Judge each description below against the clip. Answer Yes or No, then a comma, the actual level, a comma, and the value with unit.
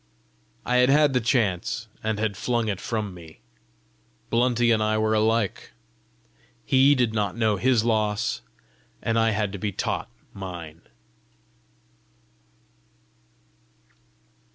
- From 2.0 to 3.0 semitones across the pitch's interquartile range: Yes, narrow, 2.6 semitones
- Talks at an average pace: No, slow, 120 wpm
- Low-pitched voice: Yes, low, 110 Hz